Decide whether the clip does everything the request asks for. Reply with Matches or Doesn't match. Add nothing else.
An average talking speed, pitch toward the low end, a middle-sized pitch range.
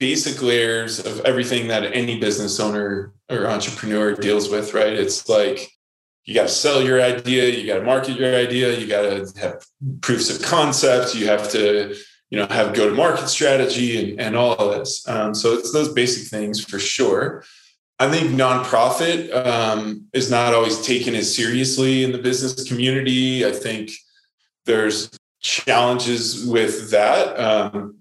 Matches